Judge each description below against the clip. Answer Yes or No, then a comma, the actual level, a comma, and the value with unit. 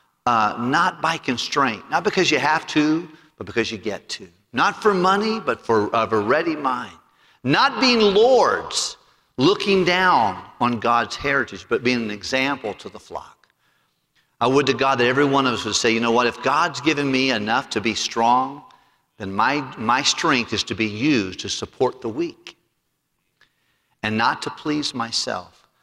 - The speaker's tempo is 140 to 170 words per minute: No, average, 180 wpm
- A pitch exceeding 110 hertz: Yes, medium, 140 Hz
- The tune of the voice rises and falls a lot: Yes, wide, 6.5 semitones